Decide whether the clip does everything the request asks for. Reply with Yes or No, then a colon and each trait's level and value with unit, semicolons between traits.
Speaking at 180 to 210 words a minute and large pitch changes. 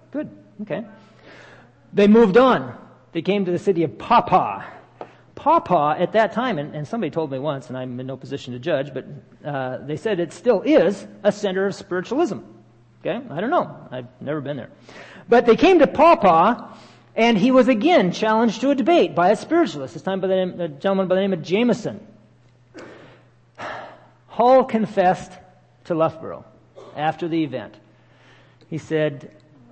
No: average, 170 wpm; wide, 7.0 semitones